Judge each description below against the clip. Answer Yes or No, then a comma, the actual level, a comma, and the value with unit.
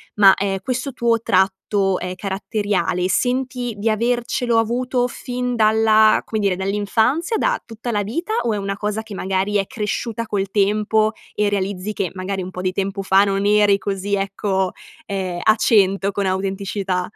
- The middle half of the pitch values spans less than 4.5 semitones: Yes, narrow, 2.6 semitones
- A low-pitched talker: No, high, 205 Hz